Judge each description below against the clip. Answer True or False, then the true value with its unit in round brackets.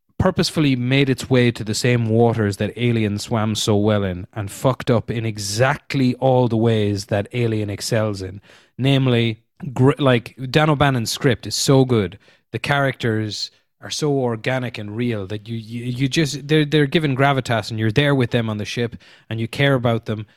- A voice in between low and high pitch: False (120 Hz)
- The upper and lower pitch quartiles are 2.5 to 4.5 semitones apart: True (3.7 semitones)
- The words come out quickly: False (185 wpm)